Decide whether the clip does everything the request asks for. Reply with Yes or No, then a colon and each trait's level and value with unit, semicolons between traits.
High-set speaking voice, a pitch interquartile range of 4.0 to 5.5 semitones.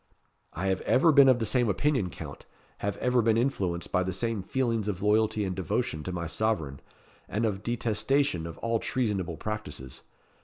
No: low, 105 Hz; average, 4.5 semitones